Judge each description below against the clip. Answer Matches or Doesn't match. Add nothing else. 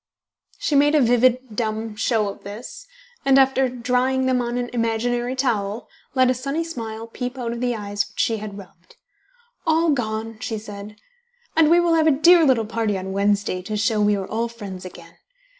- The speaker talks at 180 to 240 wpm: Matches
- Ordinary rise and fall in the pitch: Matches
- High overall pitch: Matches